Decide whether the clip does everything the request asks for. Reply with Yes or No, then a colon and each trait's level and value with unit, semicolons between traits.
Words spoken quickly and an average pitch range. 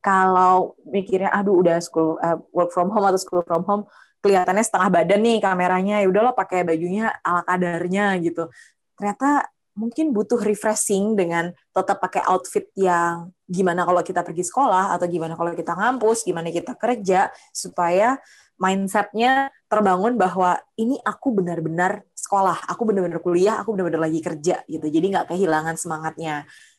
Yes: fast, 150 wpm; average, 3.3 semitones